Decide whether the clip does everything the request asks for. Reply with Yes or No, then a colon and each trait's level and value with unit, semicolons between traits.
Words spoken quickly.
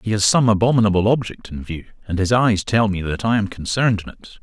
Yes: fast, 245 wpm